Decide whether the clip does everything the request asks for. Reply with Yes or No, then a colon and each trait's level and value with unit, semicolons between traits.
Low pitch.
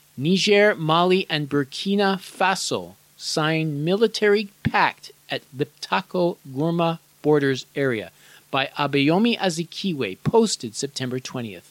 No: medium, 160 Hz